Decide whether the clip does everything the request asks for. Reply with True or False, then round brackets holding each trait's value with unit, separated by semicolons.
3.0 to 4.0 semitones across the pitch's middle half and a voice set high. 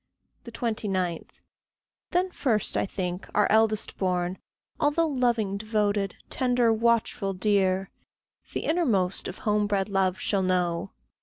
True (3.6 semitones; 205 Hz)